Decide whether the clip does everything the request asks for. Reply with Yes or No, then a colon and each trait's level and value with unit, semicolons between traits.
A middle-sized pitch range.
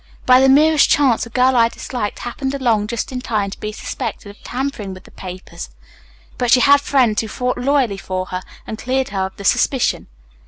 Yes: average, 4.2 semitones